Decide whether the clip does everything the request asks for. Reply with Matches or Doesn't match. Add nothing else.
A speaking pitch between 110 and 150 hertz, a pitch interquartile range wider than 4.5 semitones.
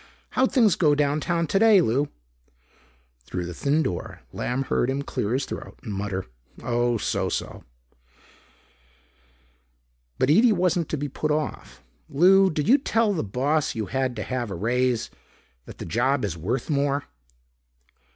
Matches